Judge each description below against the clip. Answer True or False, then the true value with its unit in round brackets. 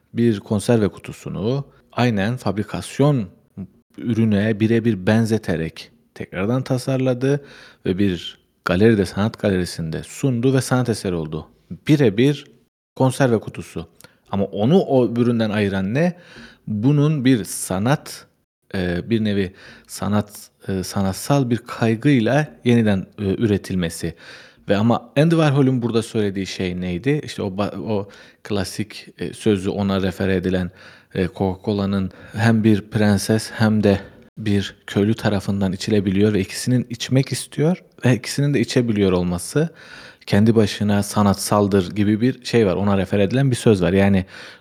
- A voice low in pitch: True (110 Hz)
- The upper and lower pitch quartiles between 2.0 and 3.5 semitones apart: False (4.2 semitones)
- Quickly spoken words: False (120 wpm)